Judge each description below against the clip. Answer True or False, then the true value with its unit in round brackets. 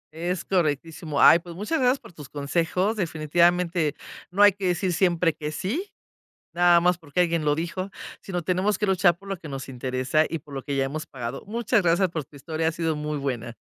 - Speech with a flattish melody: False (3.6 semitones)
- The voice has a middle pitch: True (170 Hz)